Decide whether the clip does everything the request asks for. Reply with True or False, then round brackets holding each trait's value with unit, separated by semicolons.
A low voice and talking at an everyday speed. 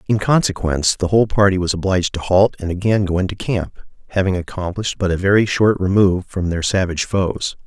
True (95 Hz; 195 wpm)